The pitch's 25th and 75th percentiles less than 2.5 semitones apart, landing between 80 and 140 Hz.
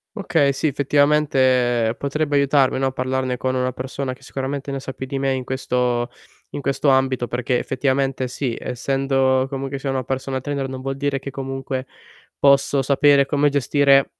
Yes: narrow, 1.2 semitones; low, 135 Hz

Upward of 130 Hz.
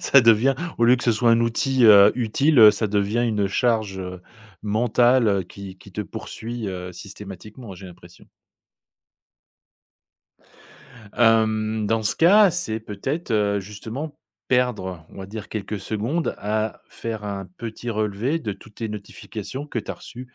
No: low, 110 Hz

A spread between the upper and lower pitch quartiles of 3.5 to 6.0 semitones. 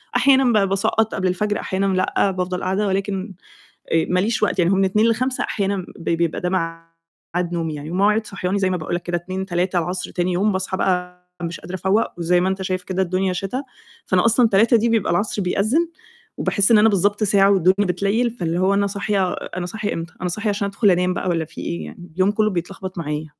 No: narrow, 2.4 semitones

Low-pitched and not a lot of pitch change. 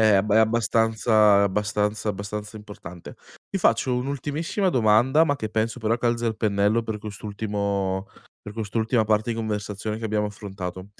Yes: low, 110 Hz; narrow, 1.8 semitones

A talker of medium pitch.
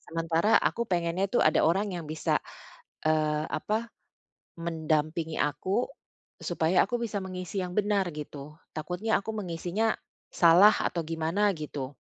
Yes: medium, 170 Hz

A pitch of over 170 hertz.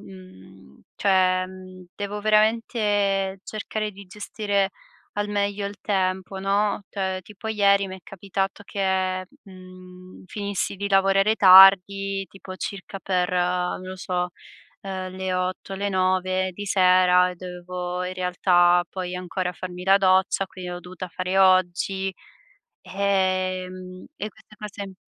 Yes: medium, 185 Hz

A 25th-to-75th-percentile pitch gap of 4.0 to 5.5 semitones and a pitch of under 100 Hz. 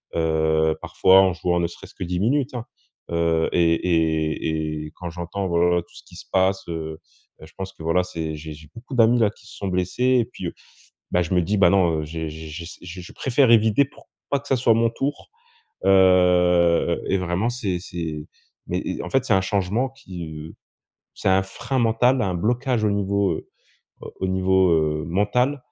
Yes: average, 4.8 semitones; very low, 90 Hz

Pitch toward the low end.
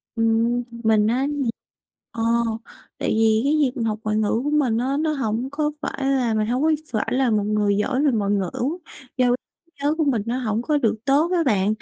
No: high, 240 Hz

